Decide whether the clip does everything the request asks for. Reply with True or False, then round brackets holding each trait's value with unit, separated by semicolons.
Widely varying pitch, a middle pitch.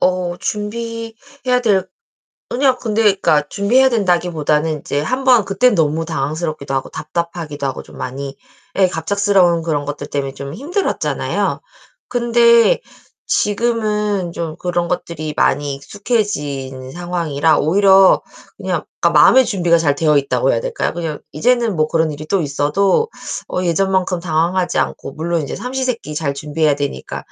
True (5.8 semitones; 175 Hz)